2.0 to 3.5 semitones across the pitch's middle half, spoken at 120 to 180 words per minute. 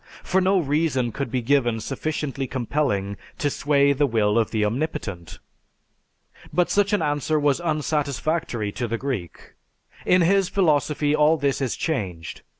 No: average, 4.9 semitones; average, 150 wpm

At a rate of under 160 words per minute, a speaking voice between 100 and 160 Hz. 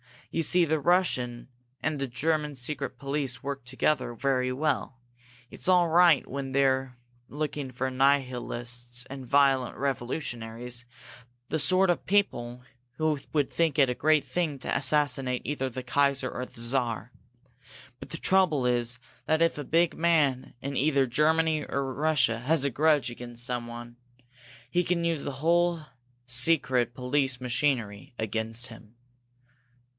Yes: average, 145 wpm; low, 135 Hz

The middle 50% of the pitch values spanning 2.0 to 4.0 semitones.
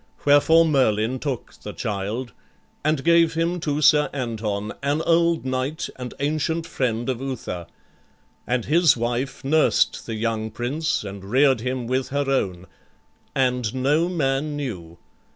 No: average, 4.7 semitones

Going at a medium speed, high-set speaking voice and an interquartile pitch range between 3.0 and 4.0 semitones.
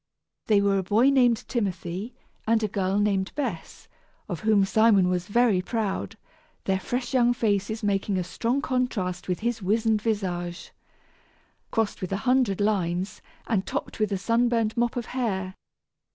Yes: average, 155 wpm; high, 210 Hz; average, 3.5 semitones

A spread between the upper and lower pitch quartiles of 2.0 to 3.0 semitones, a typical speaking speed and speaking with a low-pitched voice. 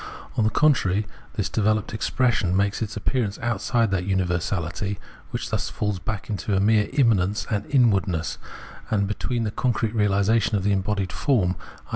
Yes: narrow, 2.5 semitones; average, 150 wpm; low, 105 Hz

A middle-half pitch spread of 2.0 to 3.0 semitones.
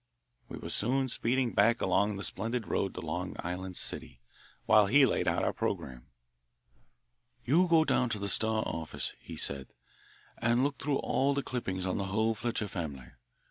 No: average, 5.2 semitones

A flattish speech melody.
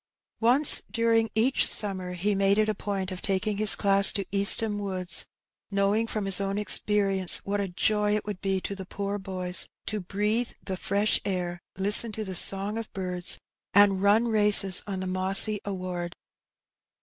Yes: narrow, 1.8 semitones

